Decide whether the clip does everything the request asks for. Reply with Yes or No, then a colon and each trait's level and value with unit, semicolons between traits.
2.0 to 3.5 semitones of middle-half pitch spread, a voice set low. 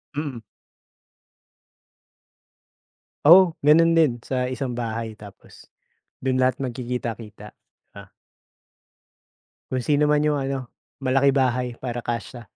Yes: average, 3.2 semitones; low, 130 Hz